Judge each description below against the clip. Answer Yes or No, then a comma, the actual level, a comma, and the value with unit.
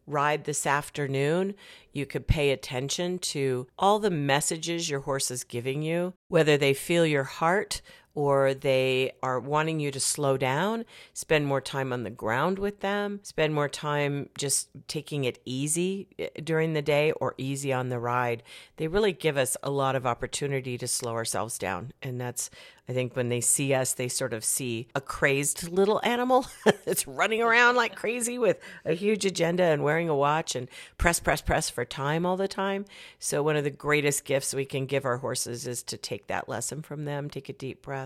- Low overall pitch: No, medium, 145 Hz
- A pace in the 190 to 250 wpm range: Yes, average, 195 wpm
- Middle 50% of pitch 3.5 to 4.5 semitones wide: Yes, average, 4.0 semitones